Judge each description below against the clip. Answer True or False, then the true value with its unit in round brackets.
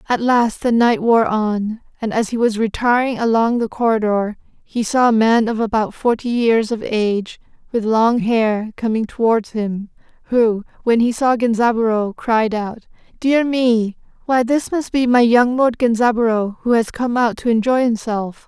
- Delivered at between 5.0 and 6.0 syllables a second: False (4.5 syllables/s)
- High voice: True (230 Hz)